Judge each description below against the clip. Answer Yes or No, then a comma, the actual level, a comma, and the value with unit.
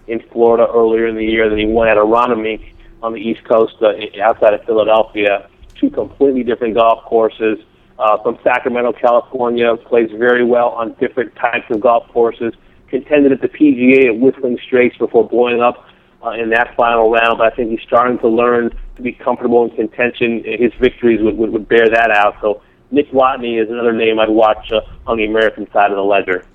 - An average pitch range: No, narrow, 1.7 semitones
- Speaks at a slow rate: No, average, 200 wpm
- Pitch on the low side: Yes, low, 115 Hz